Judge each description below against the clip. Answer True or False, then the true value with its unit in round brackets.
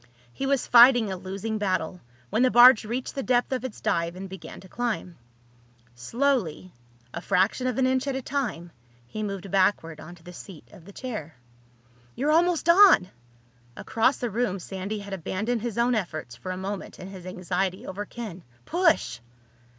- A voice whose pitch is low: False (205 Hz)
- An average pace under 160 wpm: False (175 wpm)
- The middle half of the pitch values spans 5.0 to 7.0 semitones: True (5.3 semitones)